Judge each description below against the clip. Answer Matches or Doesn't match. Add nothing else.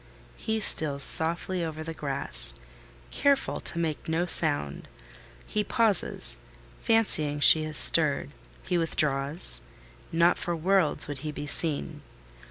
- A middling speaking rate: Doesn't match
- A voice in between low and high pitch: Matches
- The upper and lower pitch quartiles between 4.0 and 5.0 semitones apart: Doesn't match